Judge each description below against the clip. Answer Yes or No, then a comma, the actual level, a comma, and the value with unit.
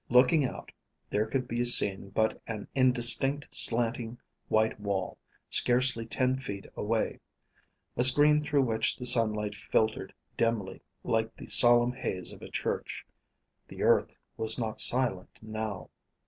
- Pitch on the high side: No, low, 115 Hz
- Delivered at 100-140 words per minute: Yes, slow, 135 wpm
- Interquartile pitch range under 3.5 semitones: Yes, narrow, 2.5 semitones